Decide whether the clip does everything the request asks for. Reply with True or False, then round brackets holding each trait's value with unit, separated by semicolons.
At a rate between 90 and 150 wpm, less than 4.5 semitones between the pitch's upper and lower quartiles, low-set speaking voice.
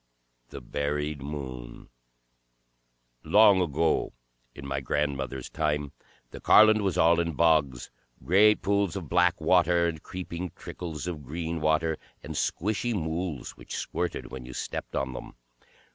True (135 wpm; 3.7 semitones; 80 Hz)